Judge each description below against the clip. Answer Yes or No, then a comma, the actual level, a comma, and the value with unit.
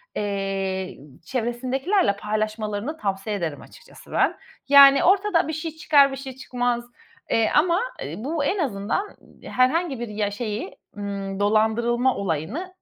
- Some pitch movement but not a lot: No, wide, 5.7 semitones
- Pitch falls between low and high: No, high, 240 Hz